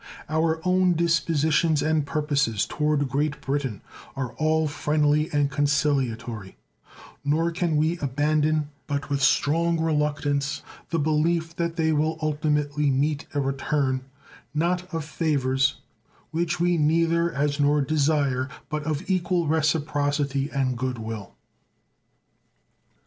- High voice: No, medium, 150 Hz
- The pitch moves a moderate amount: No, narrow, 2.2 semitones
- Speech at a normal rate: No, slow, 120 wpm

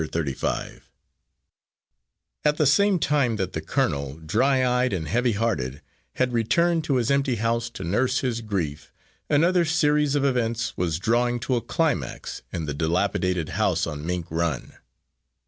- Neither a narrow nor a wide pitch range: No, wide, 8.3 semitones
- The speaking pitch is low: Yes, low, 115 Hz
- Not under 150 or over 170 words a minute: Yes, average, 155 wpm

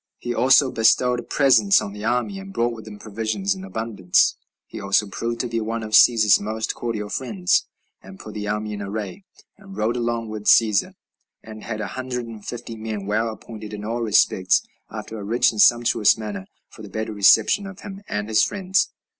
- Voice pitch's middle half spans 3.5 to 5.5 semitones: No, narrow, 2.4 semitones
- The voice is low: Yes, low, 110 Hz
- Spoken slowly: No, average, 195 wpm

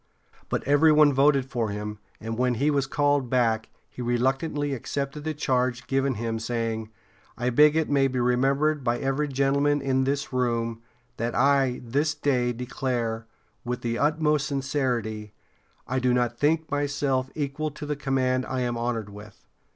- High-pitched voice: No, low, 130 Hz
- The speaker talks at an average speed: Yes, average, 165 wpm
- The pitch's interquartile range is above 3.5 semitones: No, average, 3.1 semitones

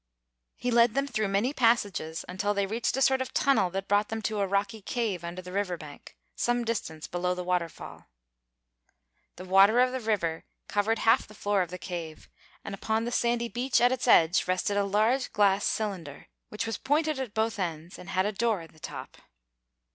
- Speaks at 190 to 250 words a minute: Yes, average, 200 wpm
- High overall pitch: Yes, high, 205 Hz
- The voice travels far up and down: No, average, 4.3 semitones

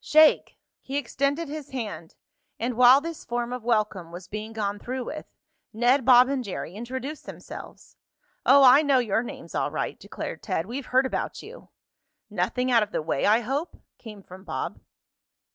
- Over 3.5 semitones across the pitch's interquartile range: Yes, average, 4.3 semitones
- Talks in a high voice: Yes, high, 245 Hz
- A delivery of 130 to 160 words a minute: No, average, 175 wpm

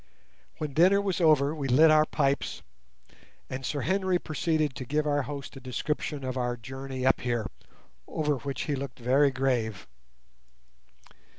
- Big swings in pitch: No, average, 2.9 semitones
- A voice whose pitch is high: No, medium, 140 Hz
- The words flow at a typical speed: Yes, average, 155 wpm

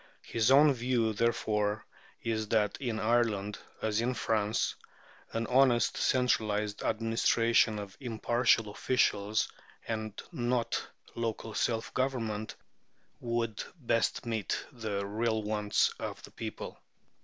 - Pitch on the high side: No, low, 115 Hz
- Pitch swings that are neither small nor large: No, narrow, 1.8 semitones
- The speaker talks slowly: Yes, slow, 110 wpm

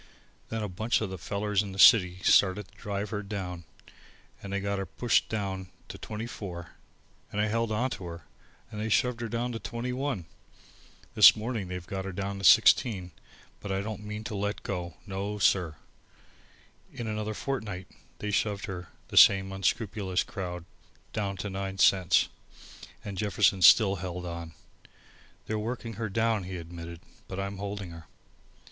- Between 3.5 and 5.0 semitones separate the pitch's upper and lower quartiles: No, narrow, 2.5 semitones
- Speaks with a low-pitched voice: Yes, low, 100 Hz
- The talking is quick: No, average, 175 wpm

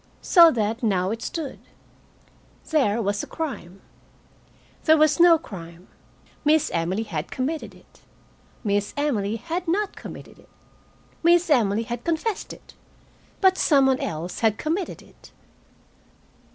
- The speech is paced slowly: Yes, slow, 130 wpm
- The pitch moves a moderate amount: No, wide, 7.9 semitones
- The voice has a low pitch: No, high, 245 Hz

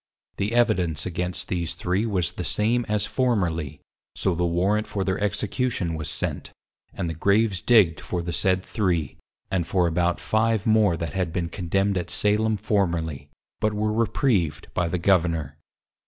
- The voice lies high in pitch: No, very low, 95 Hz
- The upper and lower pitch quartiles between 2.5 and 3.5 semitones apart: No, average, 4.0 semitones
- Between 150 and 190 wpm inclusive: Yes, average, 165 wpm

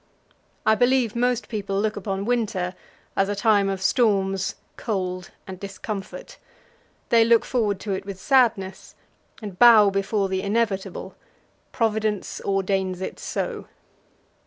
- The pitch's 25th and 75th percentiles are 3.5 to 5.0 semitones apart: No, average, 2.7 semitones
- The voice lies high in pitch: Yes, high, 200 Hz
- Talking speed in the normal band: No, slow, 130 wpm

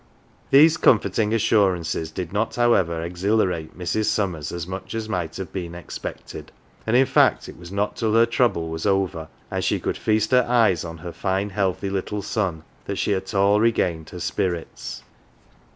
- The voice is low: Yes, very low, 95 Hz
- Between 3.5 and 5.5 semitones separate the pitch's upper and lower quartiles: Yes, average, 4.0 semitones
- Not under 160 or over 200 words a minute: Yes, average, 180 wpm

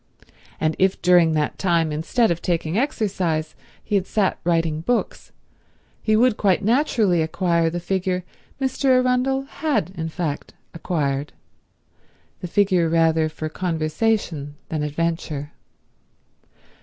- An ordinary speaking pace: No, slow, 120 wpm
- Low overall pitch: No, medium, 175 Hz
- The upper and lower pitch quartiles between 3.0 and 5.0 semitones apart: Yes, average, 4.7 semitones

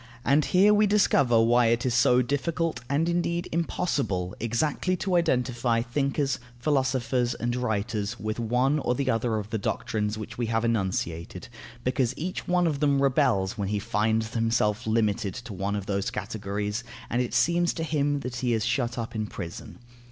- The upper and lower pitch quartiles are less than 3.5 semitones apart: No, average, 4.5 semitones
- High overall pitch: No, low, 120 Hz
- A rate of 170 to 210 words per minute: Yes, average, 175 wpm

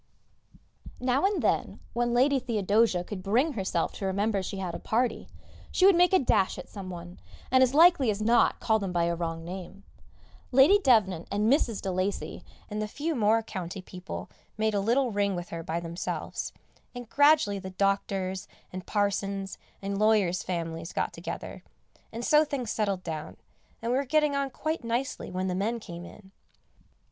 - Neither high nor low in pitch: No, high, 205 Hz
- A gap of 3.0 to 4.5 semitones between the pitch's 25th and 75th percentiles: No, average, 5.0 semitones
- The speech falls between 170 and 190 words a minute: Yes, average, 180 wpm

